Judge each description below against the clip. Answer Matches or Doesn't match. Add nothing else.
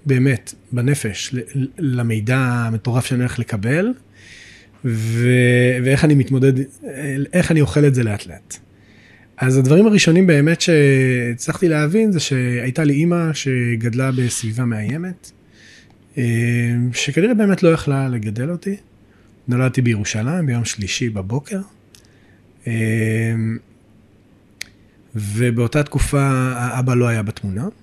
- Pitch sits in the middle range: Doesn't match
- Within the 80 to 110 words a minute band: Matches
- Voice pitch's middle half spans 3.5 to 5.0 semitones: Matches